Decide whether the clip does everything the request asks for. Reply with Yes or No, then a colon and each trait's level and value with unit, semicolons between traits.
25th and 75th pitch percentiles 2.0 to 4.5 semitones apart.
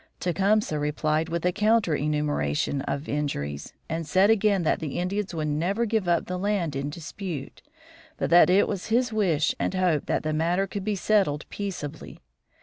No: average, 4.9 semitones